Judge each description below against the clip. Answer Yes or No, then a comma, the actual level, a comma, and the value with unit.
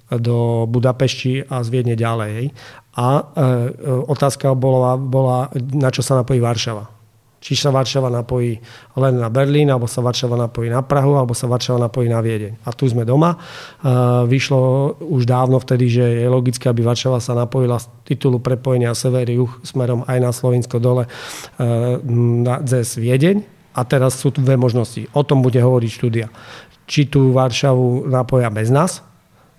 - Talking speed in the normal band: Yes, average, 155 wpm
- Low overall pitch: Yes, low, 125 Hz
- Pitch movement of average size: No, narrow, 1.7 semitones